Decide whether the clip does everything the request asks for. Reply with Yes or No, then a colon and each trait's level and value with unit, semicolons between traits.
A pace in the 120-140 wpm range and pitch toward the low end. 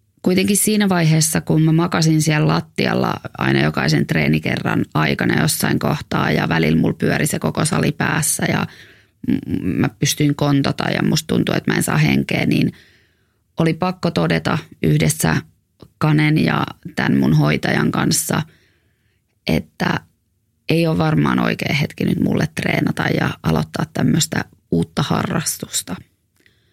No: slow, 135 wpm; medium, 150 Hz